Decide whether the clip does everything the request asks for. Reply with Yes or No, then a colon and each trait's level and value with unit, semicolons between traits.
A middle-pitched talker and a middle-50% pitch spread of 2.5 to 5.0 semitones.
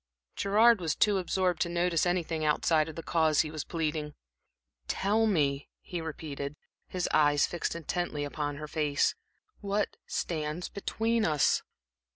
Yes: medium, 160 Hz; average, 3.3 semitones